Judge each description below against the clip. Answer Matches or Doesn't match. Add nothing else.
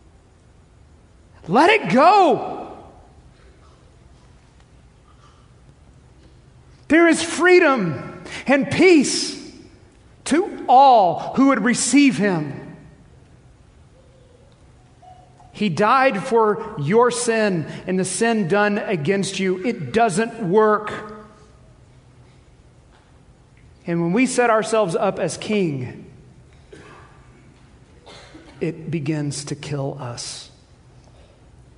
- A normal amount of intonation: Doesn't match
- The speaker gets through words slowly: Matches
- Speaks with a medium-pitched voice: Doesn't match